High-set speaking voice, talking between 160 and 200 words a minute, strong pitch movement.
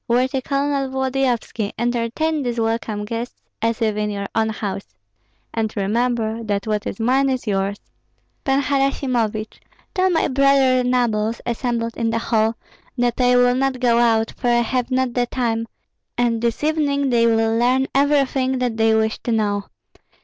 No: high, 240 Hz; average, 165 wpm; average, 2.7 semitones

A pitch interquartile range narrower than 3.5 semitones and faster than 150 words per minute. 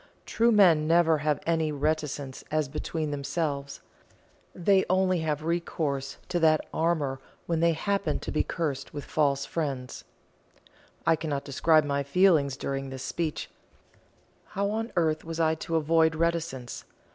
No: average, 2.9 semitones; average, 145 wpm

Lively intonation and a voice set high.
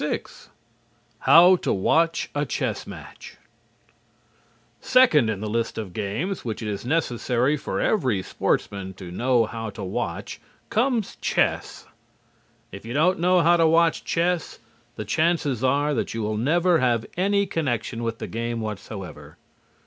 No: wide, 7.3 semitones; low, 130 Hz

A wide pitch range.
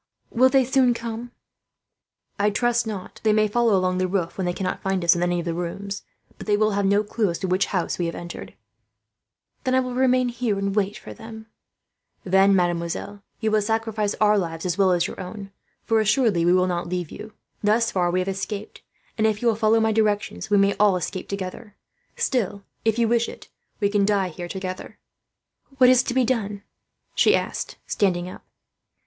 No: average, 3.3 semitones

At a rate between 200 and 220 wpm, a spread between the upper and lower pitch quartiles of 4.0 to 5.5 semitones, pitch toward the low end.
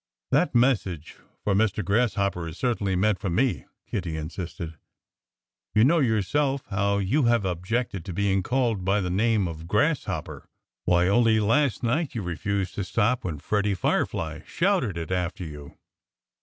No: average, 155 wpm; average, 4.6 semitones; low, 100 Hz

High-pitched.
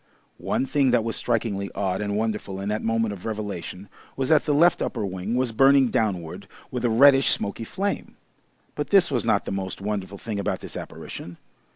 No: low, 110 Hz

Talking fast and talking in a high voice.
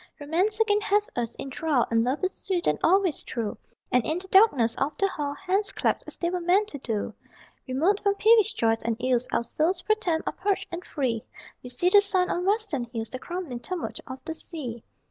Yes: fast, 220 wpm; very high, 330 Hz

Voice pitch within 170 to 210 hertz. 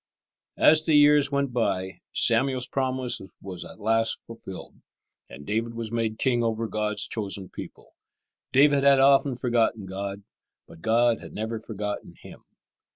No: low, 115 Hz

